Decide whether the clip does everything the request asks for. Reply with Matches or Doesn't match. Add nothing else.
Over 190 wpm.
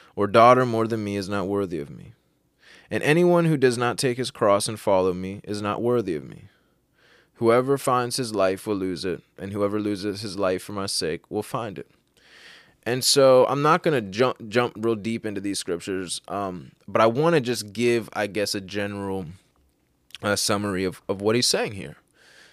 Matches